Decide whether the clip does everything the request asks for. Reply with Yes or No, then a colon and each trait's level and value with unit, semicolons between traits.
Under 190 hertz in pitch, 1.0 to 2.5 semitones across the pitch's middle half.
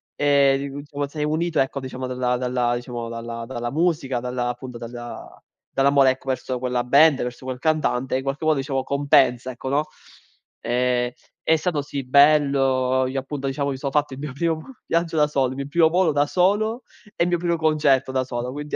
No: low, 135 Hz; average, 2.9 semitones